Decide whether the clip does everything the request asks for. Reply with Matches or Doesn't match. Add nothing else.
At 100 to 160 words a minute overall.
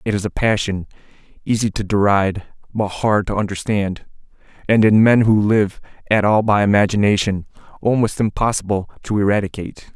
Matches